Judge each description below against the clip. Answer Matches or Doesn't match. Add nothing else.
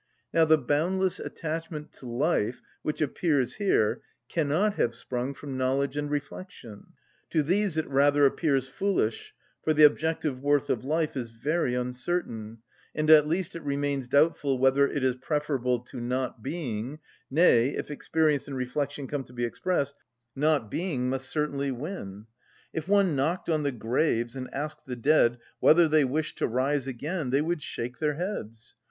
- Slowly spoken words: Doesn't match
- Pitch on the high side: Doesn't match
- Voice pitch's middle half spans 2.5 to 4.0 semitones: Matches